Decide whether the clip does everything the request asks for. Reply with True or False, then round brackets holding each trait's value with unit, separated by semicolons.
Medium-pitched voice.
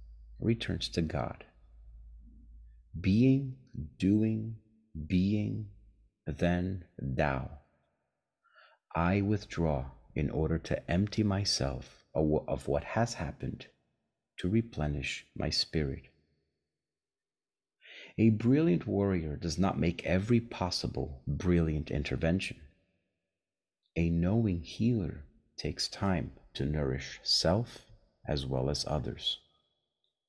False (85 Hz)